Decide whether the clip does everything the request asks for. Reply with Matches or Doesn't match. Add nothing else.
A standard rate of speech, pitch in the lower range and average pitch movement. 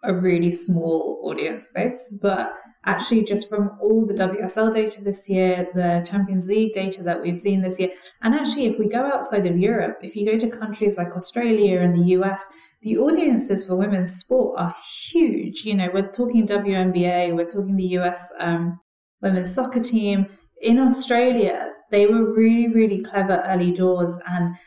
Doesn't match